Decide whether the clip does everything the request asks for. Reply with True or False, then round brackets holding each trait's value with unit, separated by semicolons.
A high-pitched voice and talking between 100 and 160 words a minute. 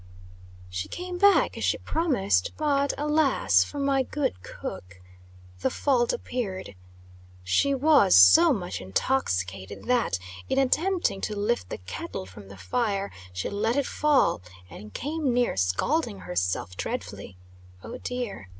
True (240 Hz; 135 wpm)